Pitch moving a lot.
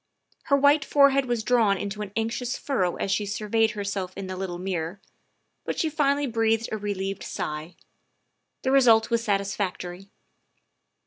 No: average, 4.3 semitones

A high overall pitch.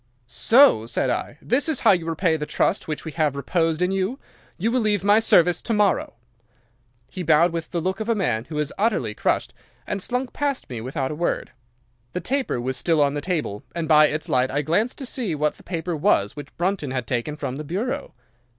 No: medium, 165 Hz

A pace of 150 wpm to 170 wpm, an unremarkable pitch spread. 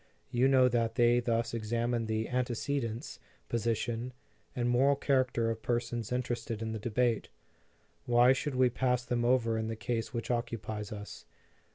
No: average, 155 wpm; narrow, 1.6 semitones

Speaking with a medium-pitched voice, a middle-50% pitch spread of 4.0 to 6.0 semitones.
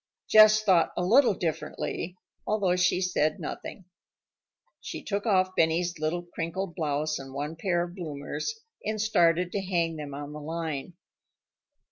No: medium, 175 Hz; average, 3.4 semitones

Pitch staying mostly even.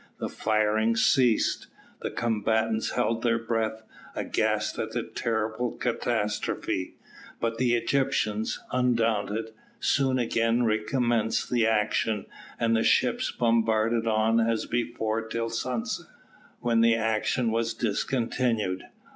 Yes: narrow, 1.2 semitones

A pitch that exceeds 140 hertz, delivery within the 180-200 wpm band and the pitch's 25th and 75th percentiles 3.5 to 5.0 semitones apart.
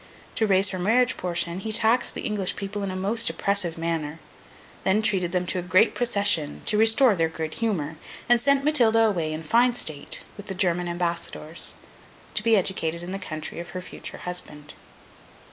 Yes: medium, 185 Hz; average, 185 wpm; average, 4.4 semitones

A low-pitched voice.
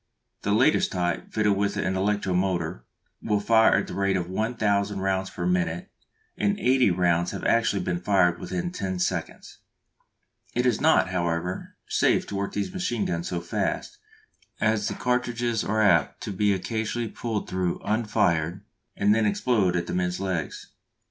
Yes: low, 100 Hz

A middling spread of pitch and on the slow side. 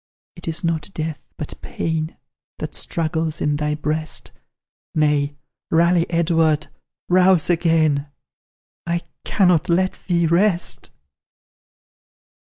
No: narrow, 1.8 semitones; slow, 100 wpm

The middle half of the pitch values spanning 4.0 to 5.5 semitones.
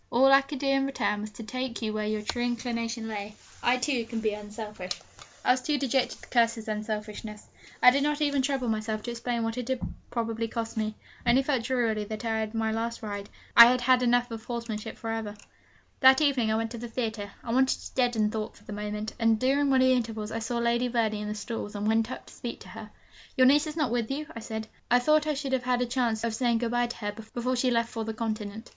No: narrow, 2.6 semitones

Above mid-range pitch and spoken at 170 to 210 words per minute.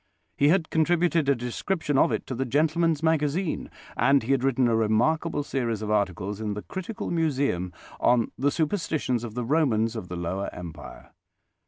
No: low, 135 Hz; average, 175 wpm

